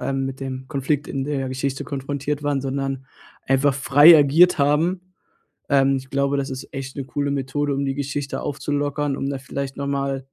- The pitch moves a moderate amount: No, narrow, 1.2 semitones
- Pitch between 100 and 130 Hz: No, medium, 140 Hz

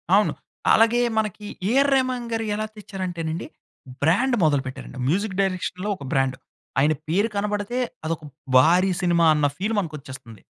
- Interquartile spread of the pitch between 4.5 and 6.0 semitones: Yes, wide, 5.5 semitones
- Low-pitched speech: No, medium, 185 Hz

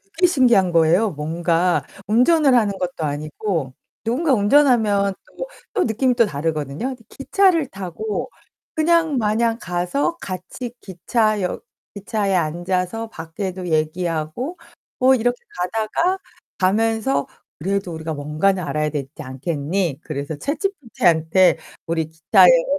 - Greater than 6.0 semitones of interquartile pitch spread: Yes, wide, 6.5 semitones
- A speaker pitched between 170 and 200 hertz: Yes, high, 190 Hz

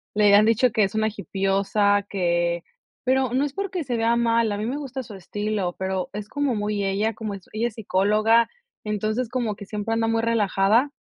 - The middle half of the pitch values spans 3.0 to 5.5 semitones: No, narrow, 2.6 semitones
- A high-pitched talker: Yes, high, 215 Hz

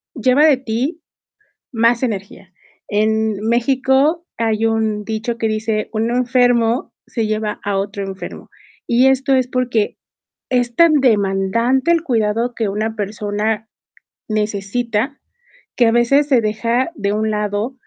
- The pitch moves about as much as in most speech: Yes, average, 3.0 semitones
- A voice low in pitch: No, high, 225 Hz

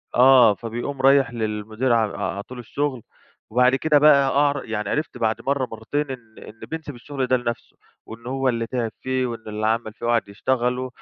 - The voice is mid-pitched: No, low, 125 Hz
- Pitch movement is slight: No, average, 3.0 semitones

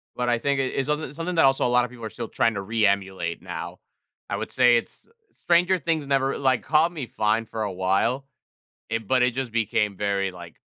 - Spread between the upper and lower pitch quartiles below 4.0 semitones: No, average, 4.5 semitones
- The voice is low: Yes, low, 120 Hz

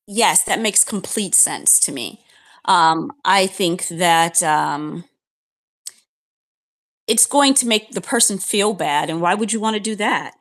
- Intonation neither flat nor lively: Yes, average, 4.4 semitones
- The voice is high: Yes, high, 200 Hz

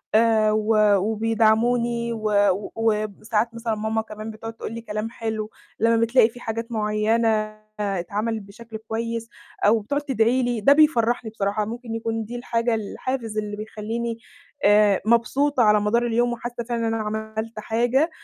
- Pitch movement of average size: No, narrow, 1.6 semitones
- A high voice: Yes, high, 225 Hz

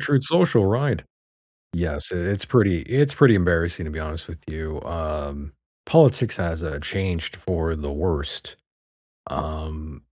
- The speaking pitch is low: Yes, very low, 85 Hz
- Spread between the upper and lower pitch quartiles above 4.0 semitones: Yes, average, 4.7 semitones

